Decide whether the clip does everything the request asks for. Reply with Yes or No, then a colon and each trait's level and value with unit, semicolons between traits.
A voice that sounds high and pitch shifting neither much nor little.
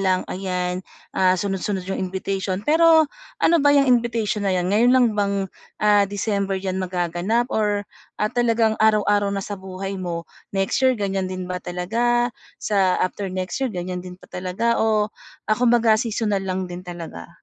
Yes: high, 195 Hz; average, 3.1 semitones